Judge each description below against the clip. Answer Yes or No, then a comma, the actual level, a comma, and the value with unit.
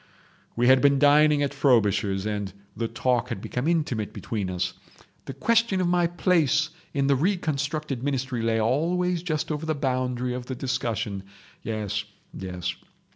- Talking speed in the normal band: Yes, average, 150 wpm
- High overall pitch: No, low, 130 Hz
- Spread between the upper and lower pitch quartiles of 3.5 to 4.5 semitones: No, wide, 5.5 semitones